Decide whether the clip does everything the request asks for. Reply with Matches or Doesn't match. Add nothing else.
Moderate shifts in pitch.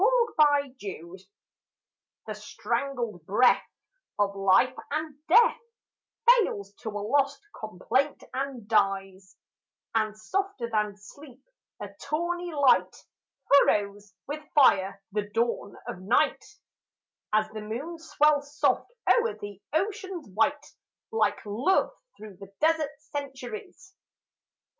Doesn't match